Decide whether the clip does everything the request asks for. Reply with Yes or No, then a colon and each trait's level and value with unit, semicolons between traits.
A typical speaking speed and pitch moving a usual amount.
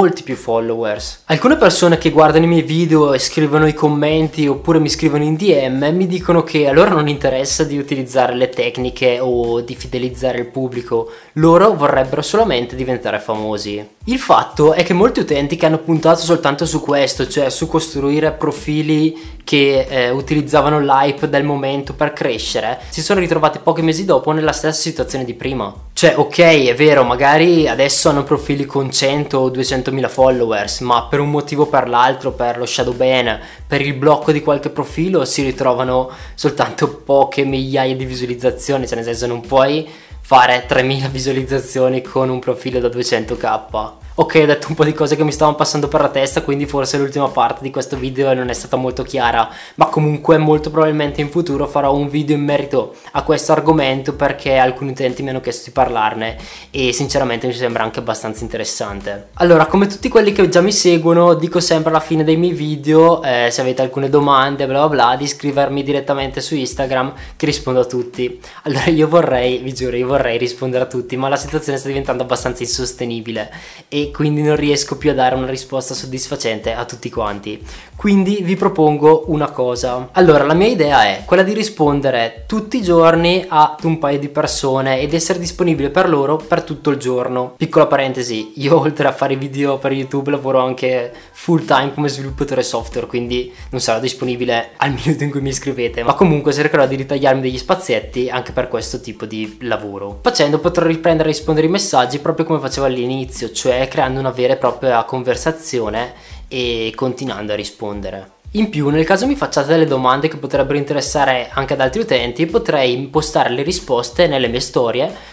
No: fast, 185 wpm; average, 3.5 semitones